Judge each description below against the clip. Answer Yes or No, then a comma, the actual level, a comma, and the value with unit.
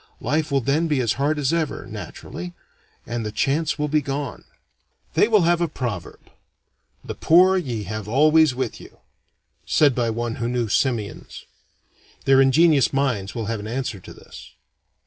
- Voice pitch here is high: No, low, 135 Hz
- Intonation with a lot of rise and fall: No, average, 5.0 semitones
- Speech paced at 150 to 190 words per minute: Yes, average, 165 wpm